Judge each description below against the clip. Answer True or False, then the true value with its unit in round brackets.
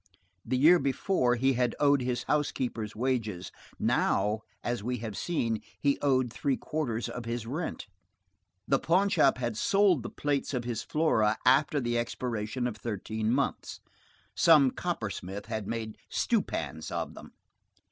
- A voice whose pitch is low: True (125 Hz)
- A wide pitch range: False (4.1 semitones)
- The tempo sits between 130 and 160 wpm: True (145 wpm)